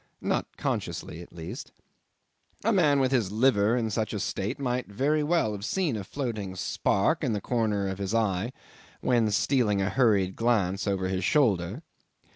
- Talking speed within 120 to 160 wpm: No, average, 170 wpm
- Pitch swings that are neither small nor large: Yes, average, 4.7 semitones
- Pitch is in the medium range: No, low, 110 Hz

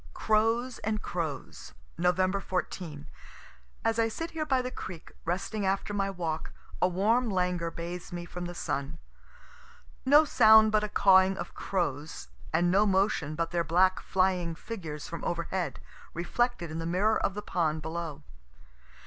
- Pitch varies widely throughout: No, average, 4.0 semitones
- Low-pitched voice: No, medium, 185 Hz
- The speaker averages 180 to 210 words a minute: No, average, 155 wpm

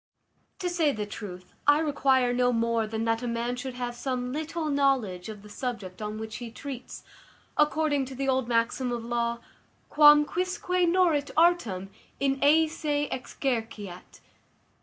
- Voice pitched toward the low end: No, very high, 250 Hz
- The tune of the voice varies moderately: Yes, average, 4.5 semitones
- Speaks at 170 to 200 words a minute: No, average, 160 wpm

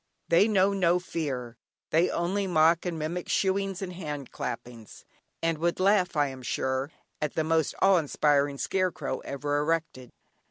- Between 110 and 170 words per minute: Yes, average, 160 wpm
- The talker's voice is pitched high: No, medium, 165 Hz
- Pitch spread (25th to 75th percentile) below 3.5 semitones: No, average, 4.1 semitones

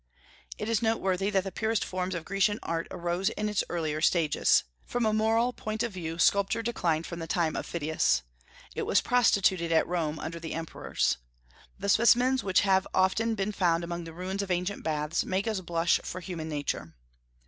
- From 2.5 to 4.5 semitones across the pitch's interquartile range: Yes, average, 4.1 semitones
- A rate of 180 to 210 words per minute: Yes, average, 190 wpm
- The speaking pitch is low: No, medium, 185 Hz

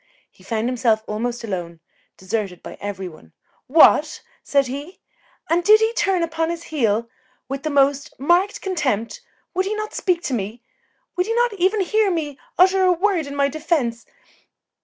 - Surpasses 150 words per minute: Yes, average, 170 wpm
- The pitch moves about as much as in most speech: No, wide, 7.9 semitones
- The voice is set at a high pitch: Yes, very high, 290 Hz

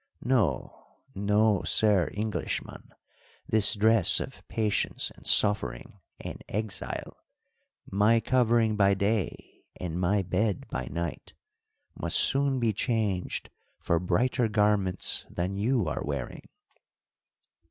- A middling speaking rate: No, slow, 110 wpm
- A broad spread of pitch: No, average, 3.3 semitones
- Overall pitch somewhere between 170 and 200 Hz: No, low, 105 Hz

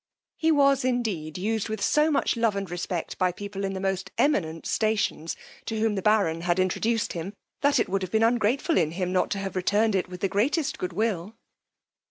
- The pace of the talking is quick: Yes, fast, 210 wpm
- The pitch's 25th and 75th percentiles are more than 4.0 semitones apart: No, average, 3.6 semitones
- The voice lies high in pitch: Yes, high, 200 Hz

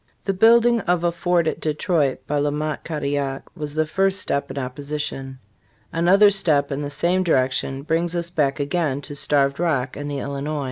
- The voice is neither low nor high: Yes, medium, 150 Hz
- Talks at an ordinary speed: Yes, average, 185 wpm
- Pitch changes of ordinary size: Yes, average, 3.6 semitones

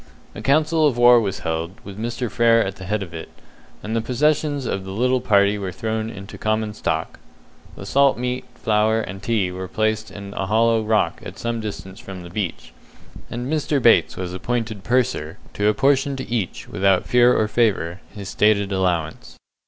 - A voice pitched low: Yes, low, 110 Hz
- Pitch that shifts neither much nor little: Yes, average, 3.9 semitones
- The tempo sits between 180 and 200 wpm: Yes, average, 185 wpm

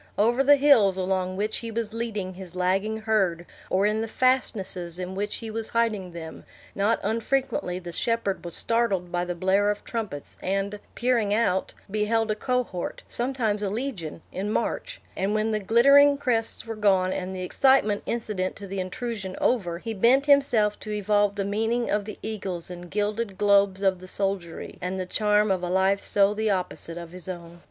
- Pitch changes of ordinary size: Yes, average, 3.4 semitones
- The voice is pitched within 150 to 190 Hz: No, high, 205 Hz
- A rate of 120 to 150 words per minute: No, average, 185 wpm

